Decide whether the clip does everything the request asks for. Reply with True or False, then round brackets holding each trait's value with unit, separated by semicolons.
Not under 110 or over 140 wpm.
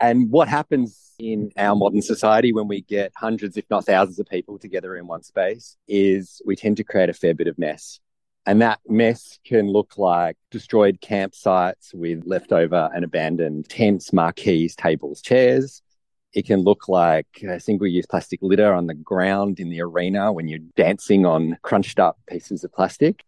False (180 wpm)